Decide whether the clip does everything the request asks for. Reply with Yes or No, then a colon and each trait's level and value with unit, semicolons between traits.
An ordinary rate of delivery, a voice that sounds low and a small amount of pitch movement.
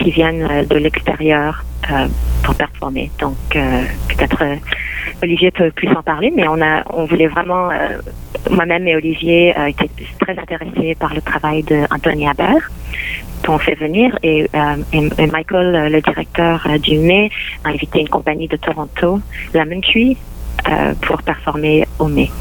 No: average, 165 wpm; medium, 160 Hz; narrow, 2.2 semitones